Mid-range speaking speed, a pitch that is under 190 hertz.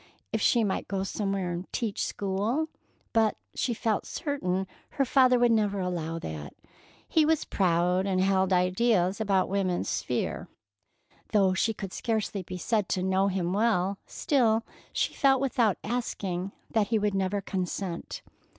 No: average, 150 wpm; high, 195 Hz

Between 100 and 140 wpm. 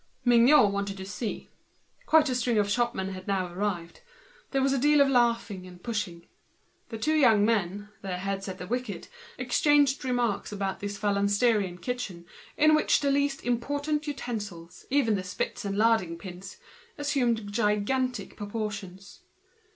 No: average, 155 wpm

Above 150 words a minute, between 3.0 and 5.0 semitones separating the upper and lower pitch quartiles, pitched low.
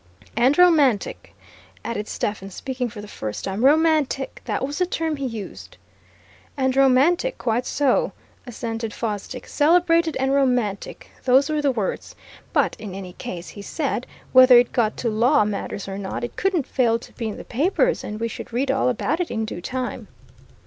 No: average, 175 wpm; average, 4.7 semitones; very high, 250 Hz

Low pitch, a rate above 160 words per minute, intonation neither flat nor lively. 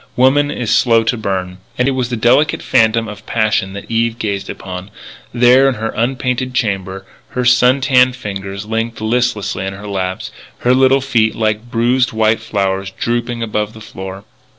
Yes: low, 115 Hz; average, 175 wpm; average, 3.8 semitones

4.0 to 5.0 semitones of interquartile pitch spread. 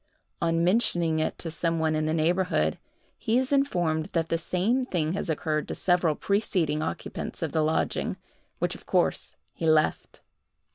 No: average, 2.7 semitones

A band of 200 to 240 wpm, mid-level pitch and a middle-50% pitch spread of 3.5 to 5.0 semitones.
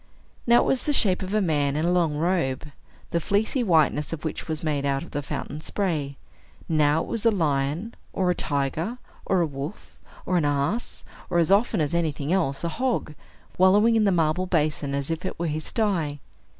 Yes: fast, 205 wpm; medium, 165 Hz; average, 4.5 semitones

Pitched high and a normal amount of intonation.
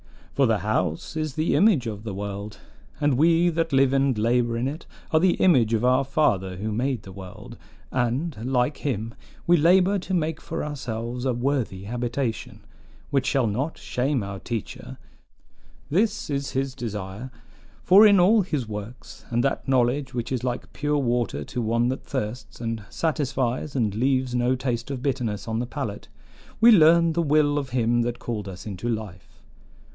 No: low, 125 Hz; average, 4.3 semitones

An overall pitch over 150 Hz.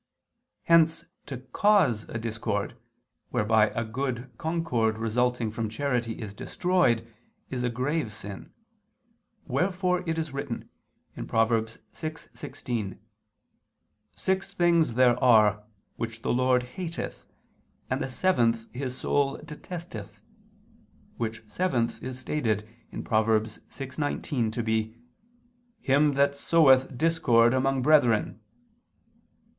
No: low, 125 Hz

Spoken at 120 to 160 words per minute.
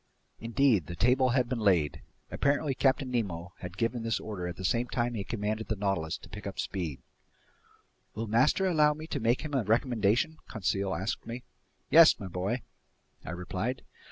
No: average, 180 wpm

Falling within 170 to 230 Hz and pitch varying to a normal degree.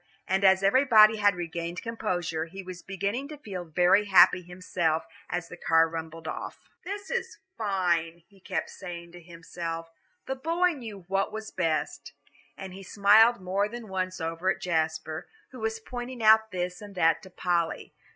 Yes: medium, 185 Hz; average, 4.1 semitones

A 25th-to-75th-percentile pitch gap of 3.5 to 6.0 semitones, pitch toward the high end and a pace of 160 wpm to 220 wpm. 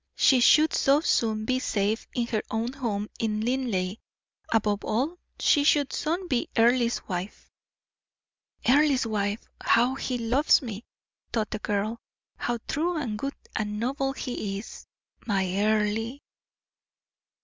No: average, 4.1 semitones; high, 235 Hz; slow, 135 wpm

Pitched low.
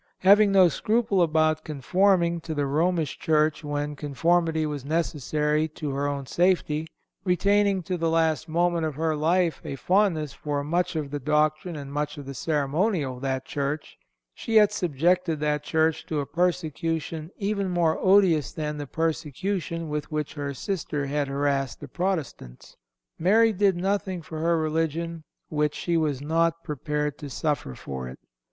No: medium, 160 Hz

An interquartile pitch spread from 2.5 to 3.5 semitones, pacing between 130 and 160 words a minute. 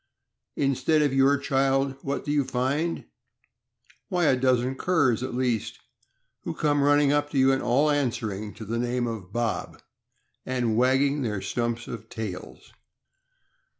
Yes: average, 3.1 semitones; average, 150 wpm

